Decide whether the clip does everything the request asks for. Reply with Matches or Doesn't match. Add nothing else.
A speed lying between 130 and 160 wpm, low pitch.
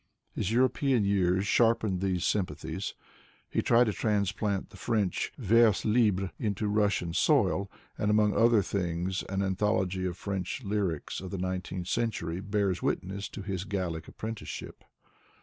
Matches